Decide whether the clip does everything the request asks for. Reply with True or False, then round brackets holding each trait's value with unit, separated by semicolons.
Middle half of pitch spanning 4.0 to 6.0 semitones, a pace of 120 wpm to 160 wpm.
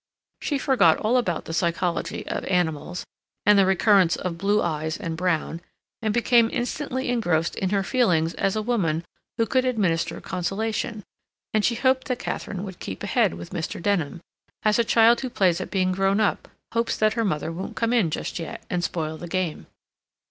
False (5.1 semitones; 185 wpm)